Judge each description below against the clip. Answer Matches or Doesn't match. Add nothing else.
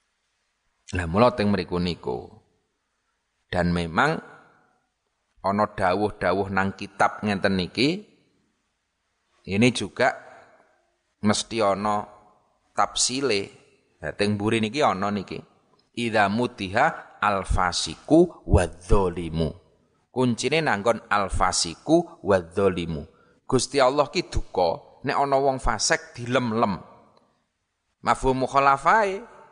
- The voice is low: Matches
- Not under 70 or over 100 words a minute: Matches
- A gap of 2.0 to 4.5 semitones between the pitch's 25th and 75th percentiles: Doesn't match